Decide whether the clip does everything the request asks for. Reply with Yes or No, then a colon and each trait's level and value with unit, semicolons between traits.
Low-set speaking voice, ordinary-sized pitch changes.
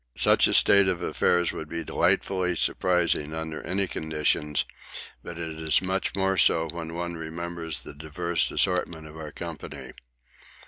No: very low, 85 Hz; narrow, 2.0 semitones